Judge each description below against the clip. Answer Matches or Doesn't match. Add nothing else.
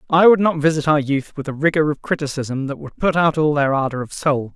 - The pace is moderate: Doesn't match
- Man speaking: Matches